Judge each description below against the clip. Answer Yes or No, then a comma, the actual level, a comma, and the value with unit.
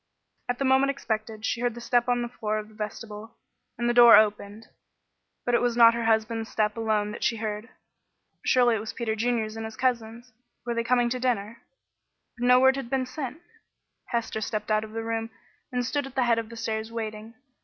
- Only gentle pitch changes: Yes, narrow, 2.0 semitones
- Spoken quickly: Yes, fast, 215 wpm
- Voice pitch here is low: No, high, 230 Hz